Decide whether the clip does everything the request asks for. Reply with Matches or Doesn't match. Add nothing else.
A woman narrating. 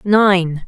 Matches